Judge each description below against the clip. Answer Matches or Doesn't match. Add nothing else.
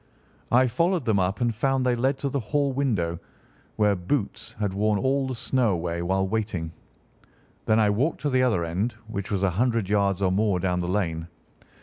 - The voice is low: Matches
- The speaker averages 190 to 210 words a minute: Matches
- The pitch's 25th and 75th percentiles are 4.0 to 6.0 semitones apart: Matches